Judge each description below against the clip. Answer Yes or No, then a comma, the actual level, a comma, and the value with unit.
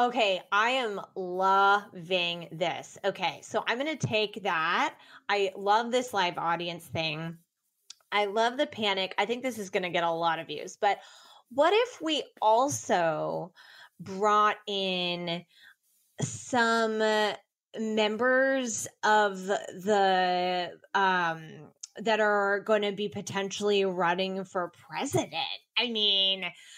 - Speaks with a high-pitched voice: Yes, high, 200 Hz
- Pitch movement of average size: Yes, average, 3.3 semitones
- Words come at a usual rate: No, slow, 125 wpm